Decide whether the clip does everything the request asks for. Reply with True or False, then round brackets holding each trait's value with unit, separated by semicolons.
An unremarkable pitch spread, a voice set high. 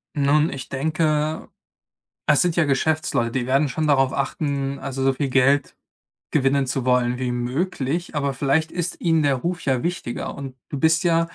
False (3.0 semitones; 140 Hz)